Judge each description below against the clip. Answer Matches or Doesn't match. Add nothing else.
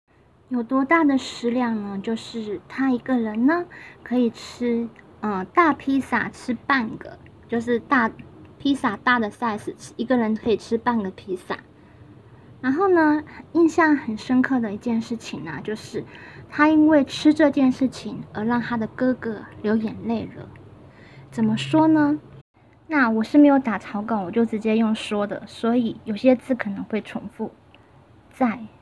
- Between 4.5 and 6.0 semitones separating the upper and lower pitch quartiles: Doesn't match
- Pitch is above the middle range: Matches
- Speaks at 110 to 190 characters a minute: Doesn't match